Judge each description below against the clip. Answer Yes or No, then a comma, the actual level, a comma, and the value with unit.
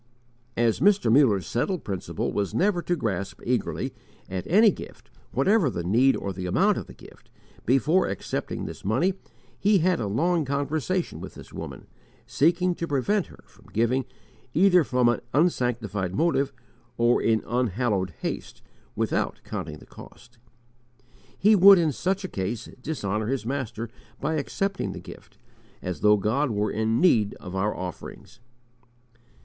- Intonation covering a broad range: Yes, wide, 8.3 semitones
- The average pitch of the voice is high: No, low, 125 Hz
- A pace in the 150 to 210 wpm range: Yes, average, 155 wpm